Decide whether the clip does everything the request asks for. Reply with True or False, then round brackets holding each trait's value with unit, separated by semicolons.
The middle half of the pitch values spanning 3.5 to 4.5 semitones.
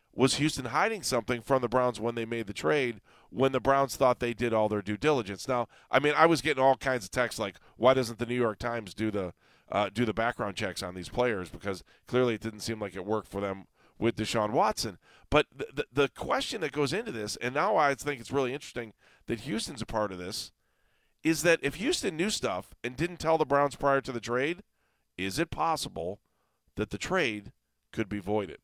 True (4.2 semitones)